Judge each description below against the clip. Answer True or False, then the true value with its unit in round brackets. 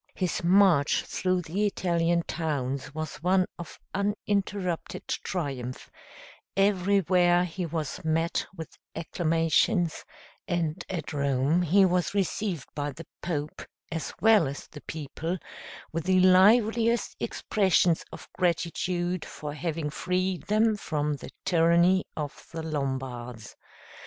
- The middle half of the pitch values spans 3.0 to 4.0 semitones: True (3.4 semitones)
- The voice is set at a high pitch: False (170 Hz)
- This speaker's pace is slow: True (115 wpm)